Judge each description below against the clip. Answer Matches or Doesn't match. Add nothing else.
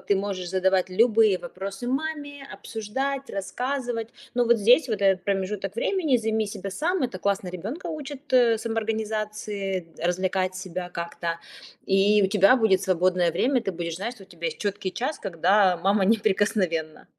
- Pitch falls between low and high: Doesn't match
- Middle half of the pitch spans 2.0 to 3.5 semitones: Doesn't match